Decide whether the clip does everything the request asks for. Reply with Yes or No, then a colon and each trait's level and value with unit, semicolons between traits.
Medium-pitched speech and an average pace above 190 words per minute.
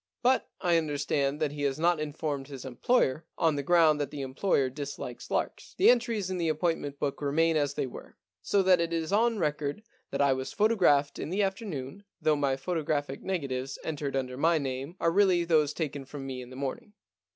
Yes: medium, 150 Hz; average, 200 wpm